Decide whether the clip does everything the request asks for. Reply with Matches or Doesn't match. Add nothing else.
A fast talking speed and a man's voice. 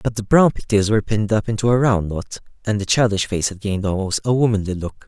Matches